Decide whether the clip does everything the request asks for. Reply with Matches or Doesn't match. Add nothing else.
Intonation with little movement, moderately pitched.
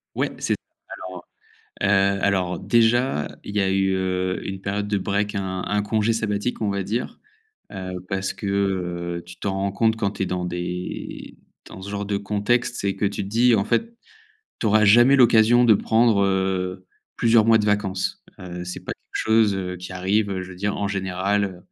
Doesn't match